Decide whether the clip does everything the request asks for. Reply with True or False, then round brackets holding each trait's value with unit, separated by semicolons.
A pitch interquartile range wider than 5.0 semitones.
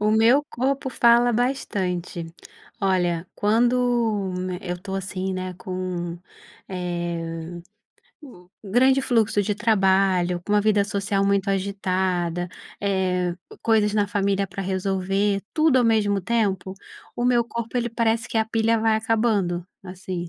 False (3.5 semitones)